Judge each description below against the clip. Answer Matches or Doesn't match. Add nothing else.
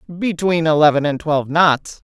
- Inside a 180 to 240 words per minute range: Doesn't match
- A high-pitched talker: Doesn't match